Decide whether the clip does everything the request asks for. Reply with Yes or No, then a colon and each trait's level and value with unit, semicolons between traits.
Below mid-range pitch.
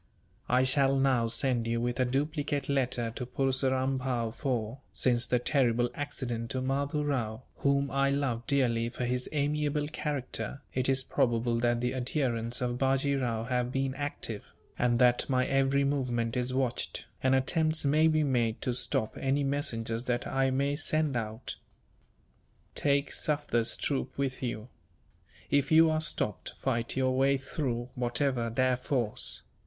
Yes: low, 130 Hz